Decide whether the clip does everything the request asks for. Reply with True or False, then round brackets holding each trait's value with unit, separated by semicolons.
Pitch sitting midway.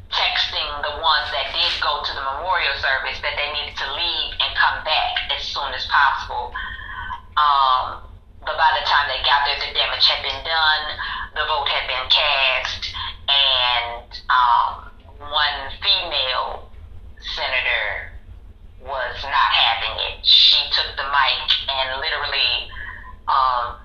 False (130 Hz)